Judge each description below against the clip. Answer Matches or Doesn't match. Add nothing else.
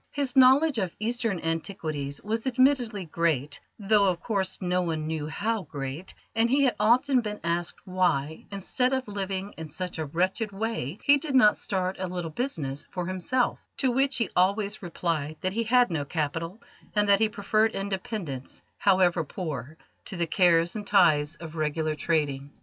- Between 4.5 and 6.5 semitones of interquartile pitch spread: Matches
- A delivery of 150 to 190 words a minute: Matches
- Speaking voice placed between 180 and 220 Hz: Matches